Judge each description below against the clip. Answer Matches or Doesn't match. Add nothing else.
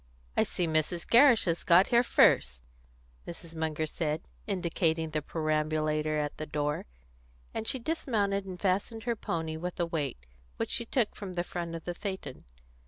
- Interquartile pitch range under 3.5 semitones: Doesn't match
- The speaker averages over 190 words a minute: Doesn't match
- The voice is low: Doesn't match